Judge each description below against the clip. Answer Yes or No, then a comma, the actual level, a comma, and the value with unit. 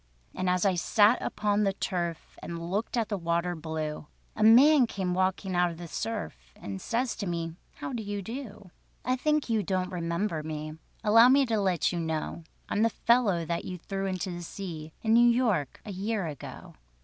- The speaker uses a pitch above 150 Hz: Yes, high, 190 Hz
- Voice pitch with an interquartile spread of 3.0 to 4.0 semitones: No, average, 4.6 semitones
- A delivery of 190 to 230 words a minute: Yes, average, 195 wpm